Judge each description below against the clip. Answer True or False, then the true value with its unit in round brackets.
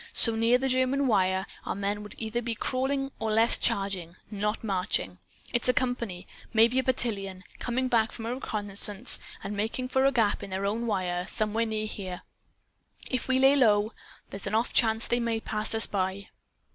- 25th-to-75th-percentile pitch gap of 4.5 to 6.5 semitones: False (3.5 semitones)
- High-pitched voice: True (220 Hz)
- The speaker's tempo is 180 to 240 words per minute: True (190 wpm)